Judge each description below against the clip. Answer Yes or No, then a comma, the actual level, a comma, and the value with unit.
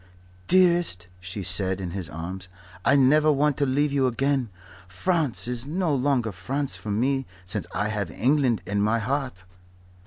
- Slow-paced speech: No, average, 160 wpm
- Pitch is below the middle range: Yes, low, 125 Hz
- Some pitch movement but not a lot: No, wide, 6.4 semitones